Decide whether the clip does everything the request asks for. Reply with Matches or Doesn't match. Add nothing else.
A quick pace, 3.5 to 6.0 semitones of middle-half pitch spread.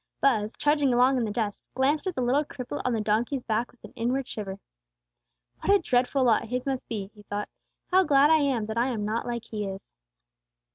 Matches